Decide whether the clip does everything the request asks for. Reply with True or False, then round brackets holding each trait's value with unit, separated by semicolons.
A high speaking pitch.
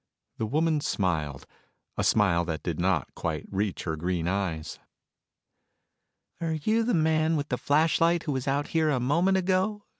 False (140 Hz)